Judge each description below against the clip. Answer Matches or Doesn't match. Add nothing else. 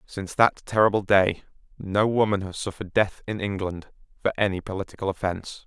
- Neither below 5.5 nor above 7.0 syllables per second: Matches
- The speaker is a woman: Doesn't match